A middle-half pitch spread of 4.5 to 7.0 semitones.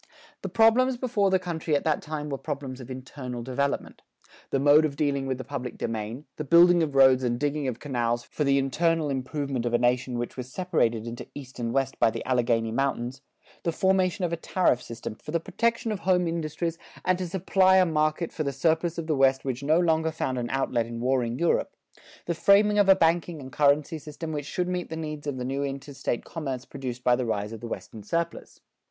Yes: average, 4.8 semitones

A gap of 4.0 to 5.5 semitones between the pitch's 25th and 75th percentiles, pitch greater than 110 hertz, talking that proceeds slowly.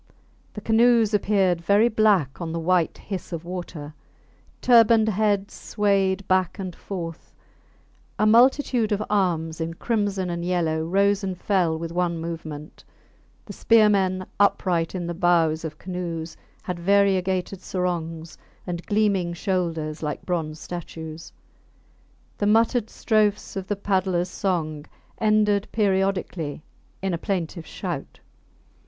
No: average, 3.4 semitones; medium, 185 Hz; slow, 125 wpm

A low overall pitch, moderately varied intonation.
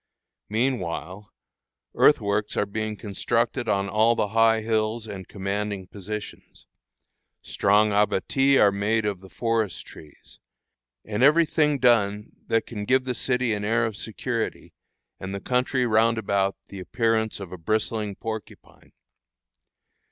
No: low, 110 Hz; narrow, 2.3 semitones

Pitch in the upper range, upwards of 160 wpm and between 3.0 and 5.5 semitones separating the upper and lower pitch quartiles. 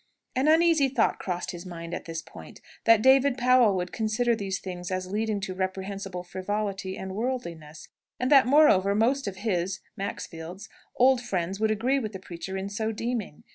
Yes: high, 200 Hz; average, 175 wpm; average, 4.7 semitones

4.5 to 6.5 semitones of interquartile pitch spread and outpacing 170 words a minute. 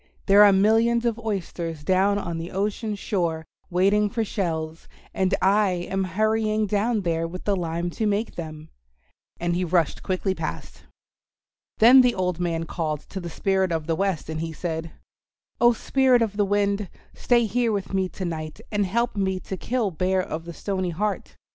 No: average, 3.6 semitones; average, 180 wpm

